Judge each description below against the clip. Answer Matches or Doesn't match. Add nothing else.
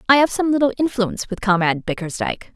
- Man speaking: Doesn't match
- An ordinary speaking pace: Matches